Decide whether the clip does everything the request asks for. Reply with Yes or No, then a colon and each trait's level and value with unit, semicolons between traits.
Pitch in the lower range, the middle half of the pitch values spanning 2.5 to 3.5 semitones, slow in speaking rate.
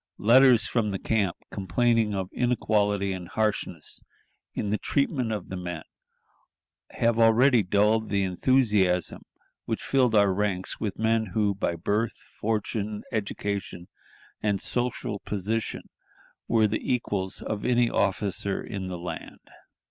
Yes: low, 105 Hz; average, 2.8 semitones; slow, 130 wpm